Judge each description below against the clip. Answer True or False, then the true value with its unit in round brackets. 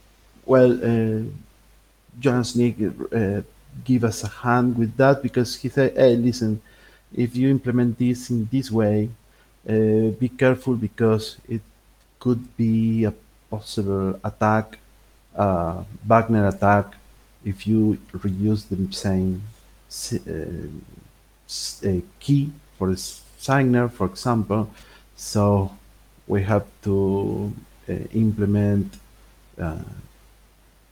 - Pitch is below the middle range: True (110 Hz)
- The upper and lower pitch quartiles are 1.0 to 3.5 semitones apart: True (3.2 semitones)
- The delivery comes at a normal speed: False (110 wpm)